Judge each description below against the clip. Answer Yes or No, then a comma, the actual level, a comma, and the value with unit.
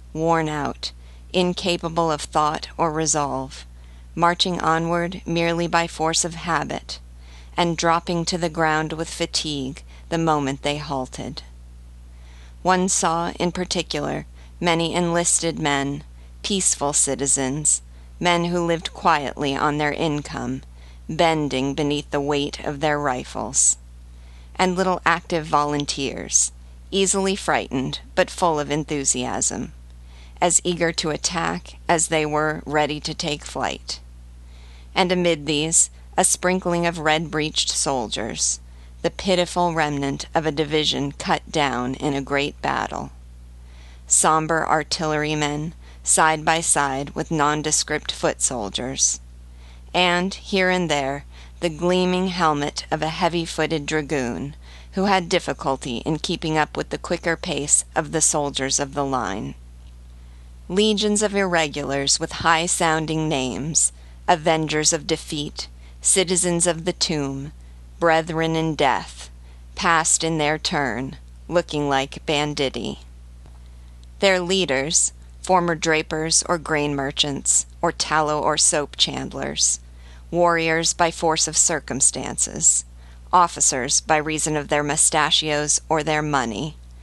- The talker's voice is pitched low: No, medium, 150 Hz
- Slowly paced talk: Yes, slow, 120 wpm